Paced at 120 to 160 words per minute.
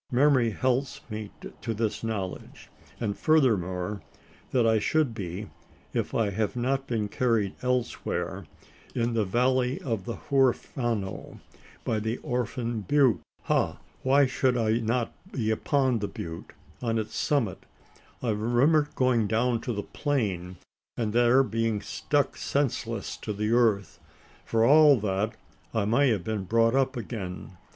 Yes: average, 145 wpm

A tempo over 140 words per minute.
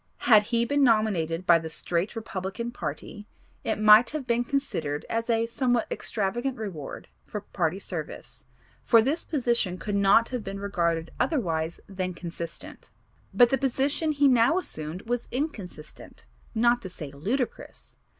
Yes: average, 150 wpm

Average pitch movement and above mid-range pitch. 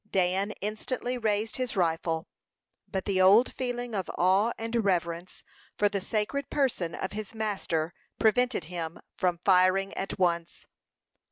Yes: average, 3.7 semitones; high, 195 Hz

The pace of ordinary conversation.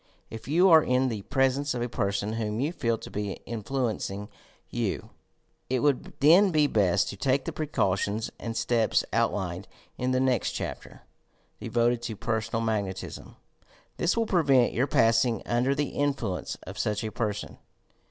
Yes: average, 170 wpm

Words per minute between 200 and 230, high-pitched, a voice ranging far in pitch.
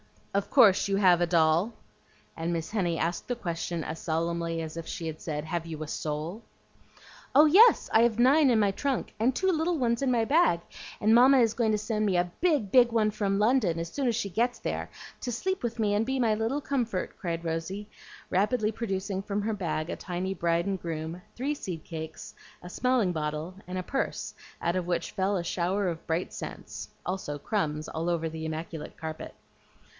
Yes: fast, 205 wpm; high, 195 Hz; wide, 5.7 semitones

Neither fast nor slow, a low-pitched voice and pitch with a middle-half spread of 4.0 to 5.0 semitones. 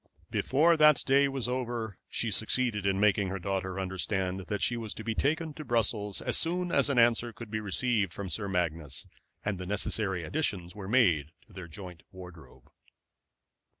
Yes: average, 180 wpm; low, 105 Hz; average, 4.5 semitones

